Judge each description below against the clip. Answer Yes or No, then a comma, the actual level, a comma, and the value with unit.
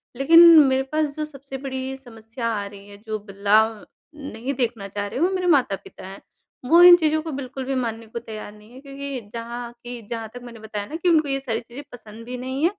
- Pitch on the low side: No, high, 245 Hz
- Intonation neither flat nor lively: Yes, average, 4.0 semitones